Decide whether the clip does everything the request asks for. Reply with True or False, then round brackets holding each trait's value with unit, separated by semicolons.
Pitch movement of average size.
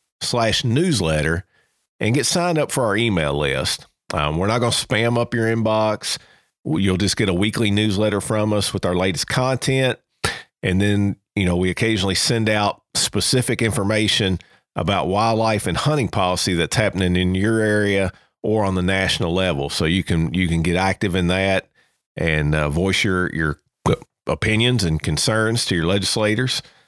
True (3.6 semitones)